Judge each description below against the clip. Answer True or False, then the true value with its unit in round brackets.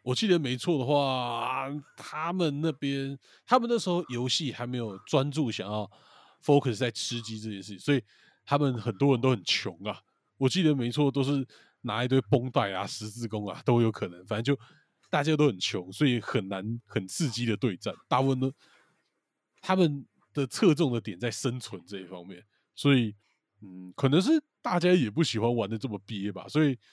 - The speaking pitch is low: True (125 Hz)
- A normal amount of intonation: True (4.8 semitones)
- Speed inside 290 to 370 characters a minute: False (280 characters per minute)